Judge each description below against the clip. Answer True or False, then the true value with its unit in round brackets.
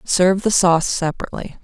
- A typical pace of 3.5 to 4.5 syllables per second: False (6.6 syllables/s)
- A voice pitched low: False (180 Hz)